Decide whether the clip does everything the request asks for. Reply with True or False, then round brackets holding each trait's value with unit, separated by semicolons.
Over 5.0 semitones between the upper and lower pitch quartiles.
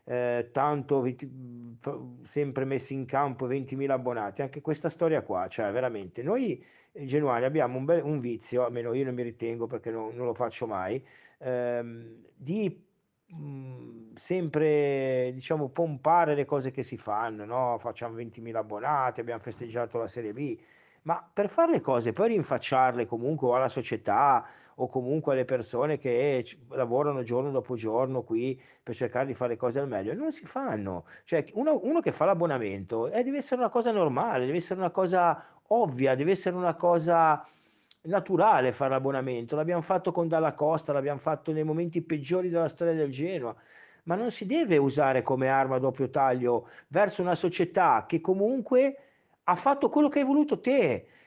True (5.6 semitones)